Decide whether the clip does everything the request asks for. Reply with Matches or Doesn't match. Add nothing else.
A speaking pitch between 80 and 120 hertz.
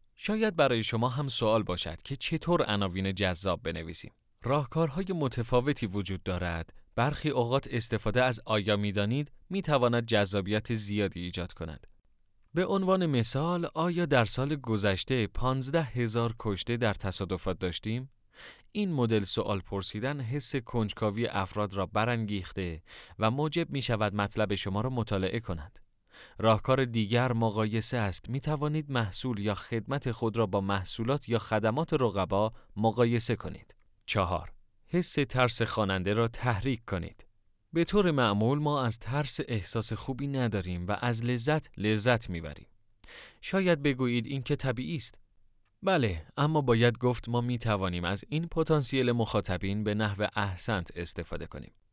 Matches